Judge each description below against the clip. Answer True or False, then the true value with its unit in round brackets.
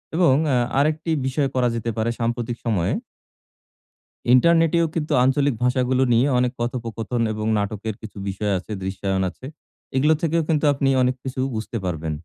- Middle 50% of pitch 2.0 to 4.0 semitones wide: False (4.4 semitones)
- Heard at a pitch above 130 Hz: False (125 Hz)